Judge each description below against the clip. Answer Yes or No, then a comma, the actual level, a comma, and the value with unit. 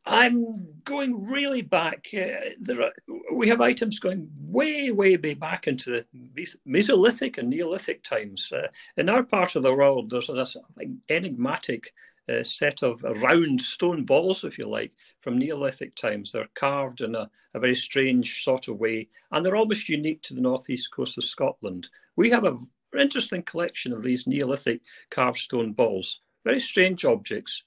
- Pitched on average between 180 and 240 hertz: Yes, medium, 185 Hz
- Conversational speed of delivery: Yes, average, 170 wpm